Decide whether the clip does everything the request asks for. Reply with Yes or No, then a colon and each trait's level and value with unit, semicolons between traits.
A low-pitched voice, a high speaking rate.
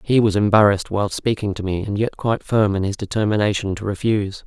Yes: low, 105 Hz; fast, 215 wpm